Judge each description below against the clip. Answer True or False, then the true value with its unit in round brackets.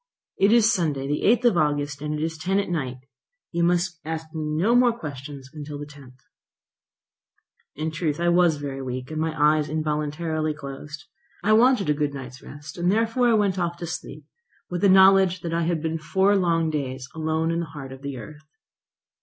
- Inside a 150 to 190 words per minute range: False (200 wpm)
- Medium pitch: True (160 Hz)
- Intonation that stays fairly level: False (3.3 semitones)